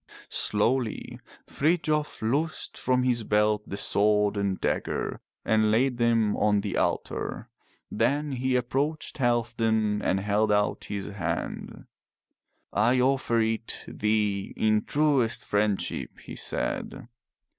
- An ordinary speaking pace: No, slow, 115 wpm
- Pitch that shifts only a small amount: No, average, 3.6 semitones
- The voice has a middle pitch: No, low, 110 Hz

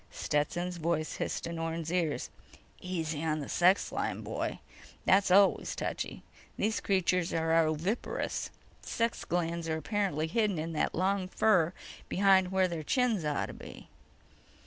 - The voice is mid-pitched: Yes, medium, 175 Hz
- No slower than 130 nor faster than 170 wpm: Yes, average, 145 wpm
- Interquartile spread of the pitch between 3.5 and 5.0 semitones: No, average, 2.9 semitones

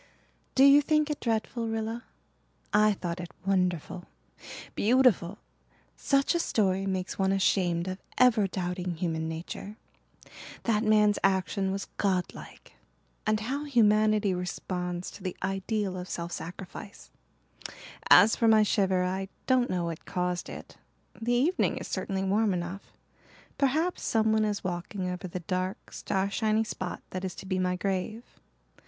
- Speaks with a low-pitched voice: No, high, 195 Hz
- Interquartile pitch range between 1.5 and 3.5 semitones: Yes, average, 3.2 semitones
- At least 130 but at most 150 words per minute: Yes, average, 140 wpm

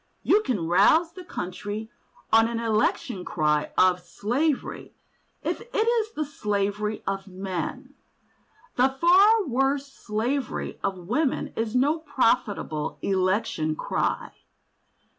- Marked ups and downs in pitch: Yes, wide, 6.8 semitones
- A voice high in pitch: Yes, high, 225 Hz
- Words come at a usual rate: No, slow, 115 wpm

